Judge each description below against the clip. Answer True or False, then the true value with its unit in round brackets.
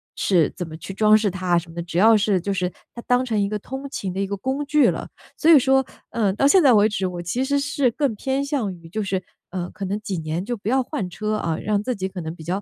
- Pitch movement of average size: False (5.9 semitones)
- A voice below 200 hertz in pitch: False (205 Hz)